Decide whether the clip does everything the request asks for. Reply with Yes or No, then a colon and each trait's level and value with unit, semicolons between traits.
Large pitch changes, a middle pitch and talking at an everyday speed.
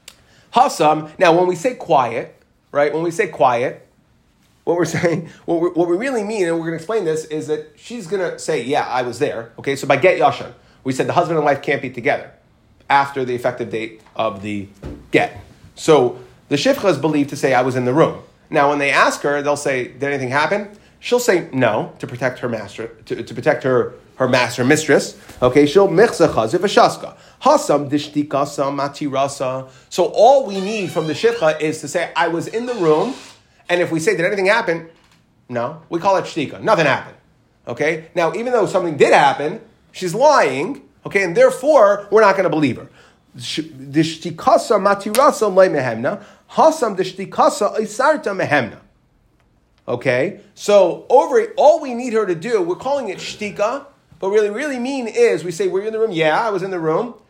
Yes: wide, 6.6 semitones; medium, 165 Hz; average, 185 wpm